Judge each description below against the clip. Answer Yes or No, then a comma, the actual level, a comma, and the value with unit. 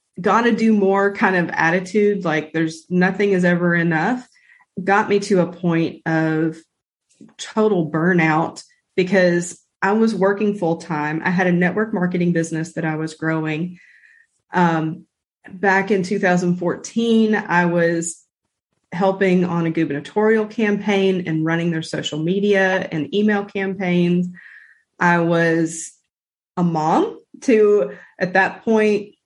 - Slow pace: Yes, slow, 130 wpm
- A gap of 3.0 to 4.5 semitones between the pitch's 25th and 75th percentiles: Yes, average, 3.7 semitones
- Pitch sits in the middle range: Yes, medium, 180 Hz